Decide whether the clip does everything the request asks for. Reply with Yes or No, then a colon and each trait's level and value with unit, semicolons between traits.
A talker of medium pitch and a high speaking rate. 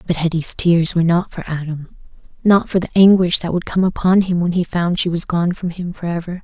Yes: medium, 175 Hz; fast, 235 wpm